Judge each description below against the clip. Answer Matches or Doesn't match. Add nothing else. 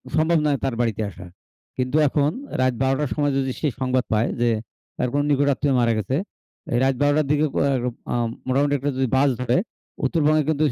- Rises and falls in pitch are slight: Matches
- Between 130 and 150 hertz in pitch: Matches